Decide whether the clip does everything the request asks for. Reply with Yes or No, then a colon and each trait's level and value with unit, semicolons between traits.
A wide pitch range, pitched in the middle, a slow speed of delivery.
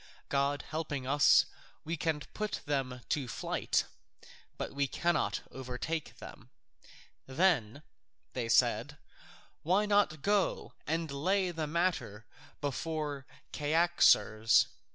No: average, 4.3 semitones; medium, 150 Hz; slow, 105 wpm